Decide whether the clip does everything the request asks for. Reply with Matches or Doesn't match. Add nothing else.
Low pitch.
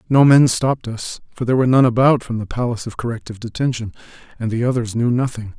Matches